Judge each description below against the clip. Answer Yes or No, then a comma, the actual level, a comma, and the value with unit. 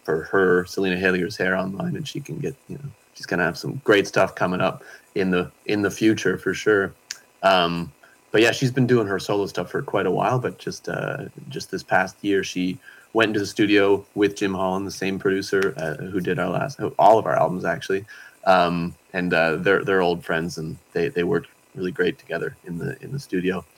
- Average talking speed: No, fast, 220 wpm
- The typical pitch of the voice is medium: No, very low, 95 Hz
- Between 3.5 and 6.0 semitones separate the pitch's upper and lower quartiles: Yes, average, 3.9 semitones